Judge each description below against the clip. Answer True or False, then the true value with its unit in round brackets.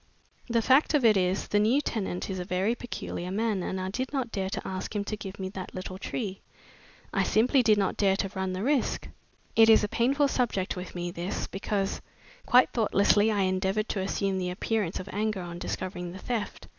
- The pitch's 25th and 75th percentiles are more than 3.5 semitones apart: False (3.1 semitones)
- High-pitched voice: True (200 Hz)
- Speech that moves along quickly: True (210 wpm)